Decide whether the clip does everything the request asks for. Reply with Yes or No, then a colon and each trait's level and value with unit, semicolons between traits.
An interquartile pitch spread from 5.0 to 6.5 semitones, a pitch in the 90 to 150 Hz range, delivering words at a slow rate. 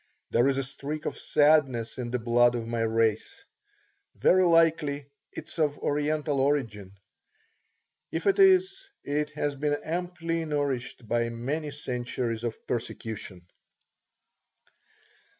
No: average, 4.6 semitones; medium, 140 Hz; slow, 125 wpm